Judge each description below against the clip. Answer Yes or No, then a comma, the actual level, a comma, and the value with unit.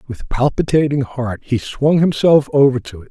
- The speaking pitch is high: No, low, 135 Hz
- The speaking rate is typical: Yes, average, 175 wpm